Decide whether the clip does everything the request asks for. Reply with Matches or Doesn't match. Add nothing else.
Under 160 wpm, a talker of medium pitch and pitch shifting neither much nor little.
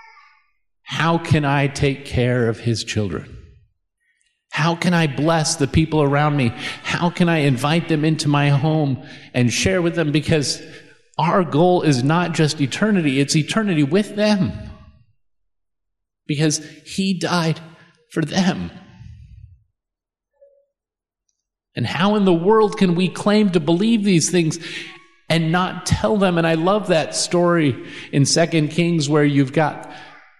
Matches